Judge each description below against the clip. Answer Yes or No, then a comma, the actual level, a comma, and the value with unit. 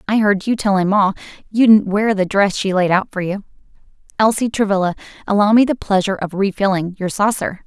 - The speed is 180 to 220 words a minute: Yes, average, 195 wpm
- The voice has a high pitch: Yes, high, 200 Hz